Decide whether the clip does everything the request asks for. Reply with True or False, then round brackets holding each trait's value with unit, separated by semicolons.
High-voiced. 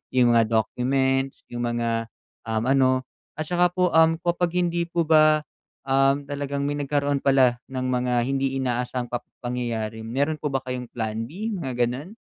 False (135 Hz)